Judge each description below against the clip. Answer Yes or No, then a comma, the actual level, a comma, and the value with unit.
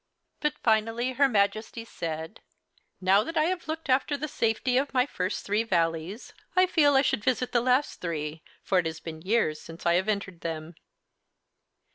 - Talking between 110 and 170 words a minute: No, average, 180 wpm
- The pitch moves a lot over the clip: Yes, wide, 7.4 semitones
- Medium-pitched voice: No, high, 220 Hz